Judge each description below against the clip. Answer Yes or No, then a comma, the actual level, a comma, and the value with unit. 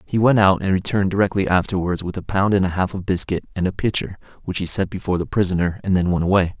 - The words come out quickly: Yes, fast, 255 wpm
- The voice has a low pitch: Yes, very low, 95 Hz